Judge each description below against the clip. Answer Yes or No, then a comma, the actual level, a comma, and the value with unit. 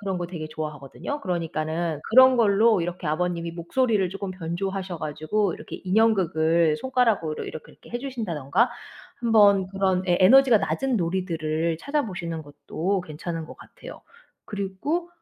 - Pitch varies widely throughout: No, average, 4.9 semitones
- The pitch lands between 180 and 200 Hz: Yes, medium, 185 Hz